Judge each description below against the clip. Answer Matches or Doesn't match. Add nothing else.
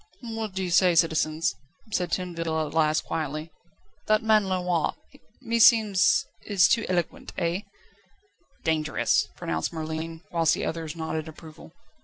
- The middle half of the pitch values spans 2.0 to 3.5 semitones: Matches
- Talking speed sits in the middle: Doesn't match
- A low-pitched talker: Doesn't match